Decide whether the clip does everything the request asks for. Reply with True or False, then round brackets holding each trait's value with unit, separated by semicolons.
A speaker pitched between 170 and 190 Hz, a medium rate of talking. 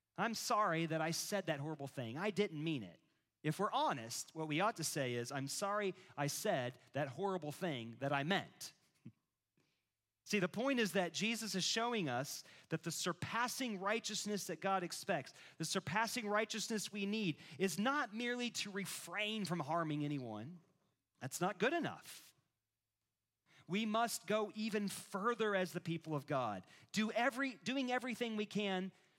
True (185 Hz; 165 wpm)